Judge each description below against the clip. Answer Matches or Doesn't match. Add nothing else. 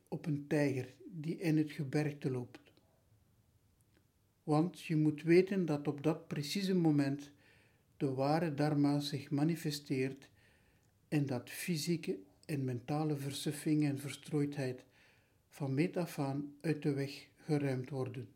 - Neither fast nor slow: Doesn't match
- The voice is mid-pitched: Matches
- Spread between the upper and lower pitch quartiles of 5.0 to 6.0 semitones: Doesn't match